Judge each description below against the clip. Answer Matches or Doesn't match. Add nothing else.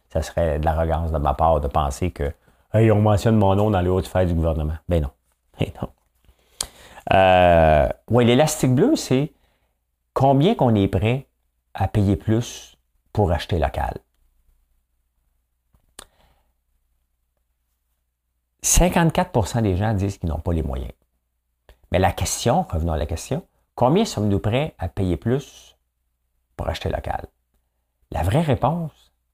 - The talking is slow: Matches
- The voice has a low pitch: Matches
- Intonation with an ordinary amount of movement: Doesn't match